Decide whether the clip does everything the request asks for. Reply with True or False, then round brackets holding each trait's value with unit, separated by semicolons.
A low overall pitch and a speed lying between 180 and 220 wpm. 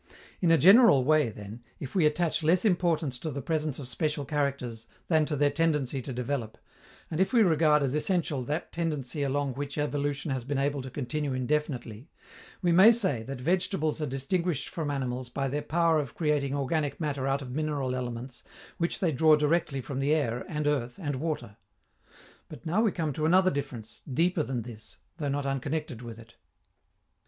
False (145 Hz; 185 wpm)